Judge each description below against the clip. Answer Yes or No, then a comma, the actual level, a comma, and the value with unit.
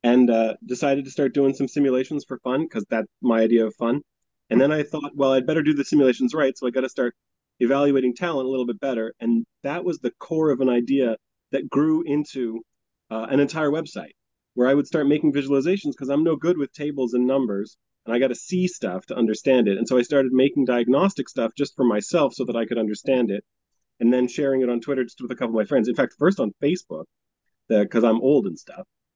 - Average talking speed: No, fast, 235 wpm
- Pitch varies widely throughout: No, average, 2.9 semitones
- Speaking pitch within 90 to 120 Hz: No, low, 130 Hz